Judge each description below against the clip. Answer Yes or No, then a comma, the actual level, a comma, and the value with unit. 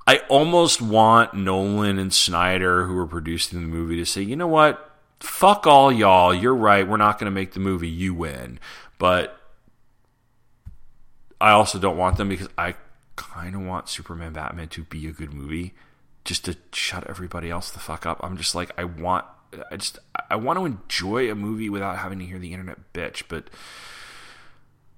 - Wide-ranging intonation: No, average, 4.1 semitones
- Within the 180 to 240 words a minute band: Yes, average, 185 wpm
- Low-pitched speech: Yes, very low, 95 Hz